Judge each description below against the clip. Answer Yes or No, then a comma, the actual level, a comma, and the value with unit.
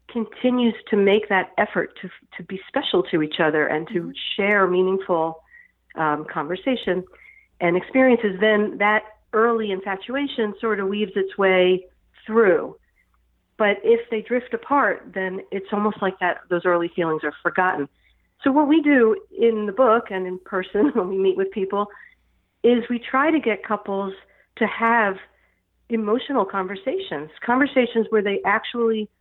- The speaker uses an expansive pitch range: No, average, 3.6 semitones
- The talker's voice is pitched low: No, high, 205 Hz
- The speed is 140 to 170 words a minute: Yes, average, 150 wpm